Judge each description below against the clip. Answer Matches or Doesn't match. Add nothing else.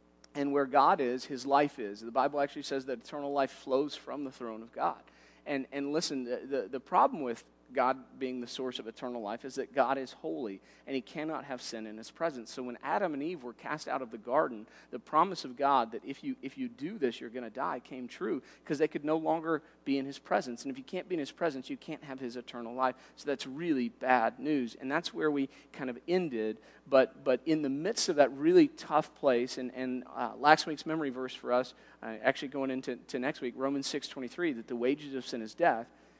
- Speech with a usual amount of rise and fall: Matches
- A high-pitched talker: Doesn't match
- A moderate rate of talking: Doesn't match